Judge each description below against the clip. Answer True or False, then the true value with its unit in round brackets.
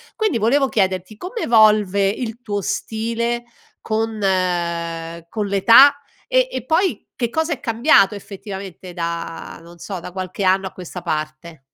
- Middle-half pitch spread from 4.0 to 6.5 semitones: True (4.5 semitones)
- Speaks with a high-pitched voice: True (200 Hz)